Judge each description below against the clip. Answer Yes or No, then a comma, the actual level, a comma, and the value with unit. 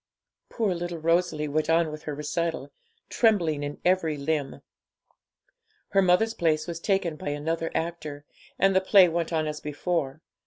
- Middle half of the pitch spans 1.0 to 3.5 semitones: Yes, average, 2.7 semitones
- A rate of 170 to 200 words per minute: No, average, 155 wpm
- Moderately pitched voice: Yes, medium, 165 Hz